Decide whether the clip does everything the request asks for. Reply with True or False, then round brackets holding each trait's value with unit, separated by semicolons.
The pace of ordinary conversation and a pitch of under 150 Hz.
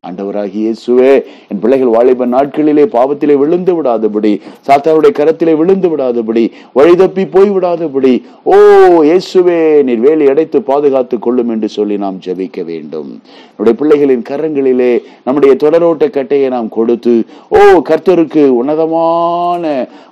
True (115 wpm; 140 Hz)